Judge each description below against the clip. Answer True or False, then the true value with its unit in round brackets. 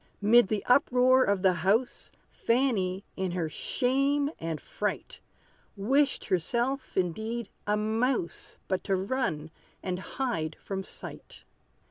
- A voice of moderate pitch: False (215 Hz)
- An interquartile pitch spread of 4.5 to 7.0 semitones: True (5.6 semitones)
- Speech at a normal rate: False (120 wpm)